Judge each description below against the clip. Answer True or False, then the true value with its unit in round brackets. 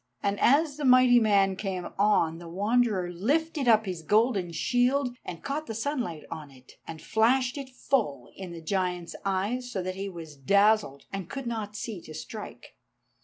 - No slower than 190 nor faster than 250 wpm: False (175 wpm)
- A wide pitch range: True (5.7 semitones)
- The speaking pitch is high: True (205 Hz)